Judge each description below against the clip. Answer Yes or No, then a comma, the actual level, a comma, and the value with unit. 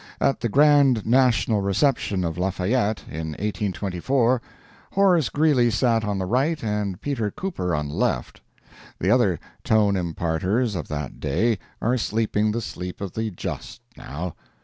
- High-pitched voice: No, low, 105 Hz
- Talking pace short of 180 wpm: Yes, average, 150 wpm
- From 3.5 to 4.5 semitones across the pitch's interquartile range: No, wide, 5.5 semitones